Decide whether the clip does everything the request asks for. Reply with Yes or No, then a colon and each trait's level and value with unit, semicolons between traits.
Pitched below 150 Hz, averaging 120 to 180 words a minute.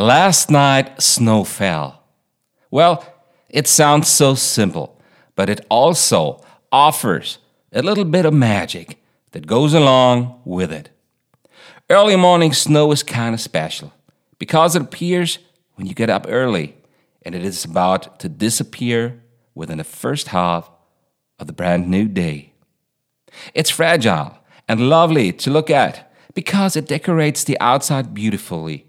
Yes: low, 135 Hz; slow, 135 wpm